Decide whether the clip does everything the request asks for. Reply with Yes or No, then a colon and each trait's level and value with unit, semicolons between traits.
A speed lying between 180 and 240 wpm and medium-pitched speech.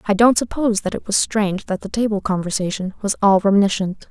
No: fast, 205 wpm; high, 205 Hz